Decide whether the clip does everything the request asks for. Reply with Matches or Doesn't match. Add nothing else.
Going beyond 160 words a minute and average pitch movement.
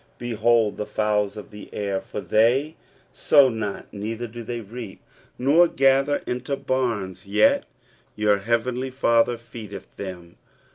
Doesn't match